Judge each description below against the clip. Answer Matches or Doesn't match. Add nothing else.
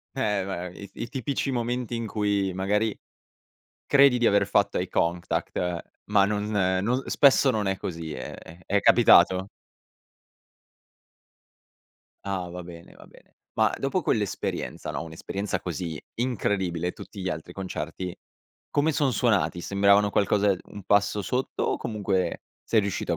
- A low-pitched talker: Matches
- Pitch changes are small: Doesn't match